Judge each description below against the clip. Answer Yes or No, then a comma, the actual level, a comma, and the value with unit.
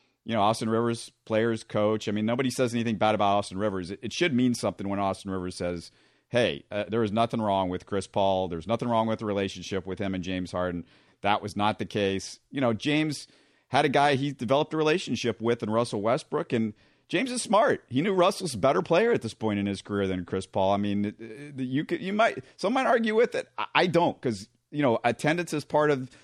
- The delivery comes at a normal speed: No, fast, 235 wpm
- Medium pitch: No, low, 110 Hz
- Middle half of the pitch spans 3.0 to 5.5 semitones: Yes, average, 4.7 semitones